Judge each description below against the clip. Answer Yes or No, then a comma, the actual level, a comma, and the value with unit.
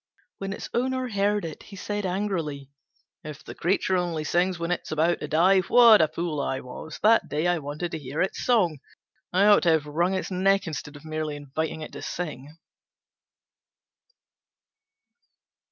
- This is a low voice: No, medium, 170 Hz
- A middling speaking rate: Yes, average, 175 wpm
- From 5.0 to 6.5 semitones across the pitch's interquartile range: No, average, 4.2 semitones